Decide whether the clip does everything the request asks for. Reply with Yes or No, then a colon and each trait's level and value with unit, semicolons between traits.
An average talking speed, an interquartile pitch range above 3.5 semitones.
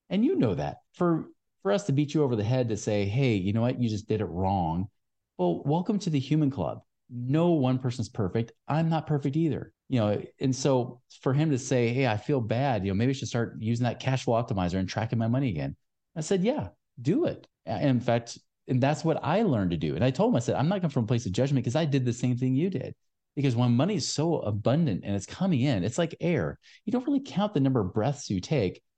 No: fast, 260 wpm; average, 5.1 semitones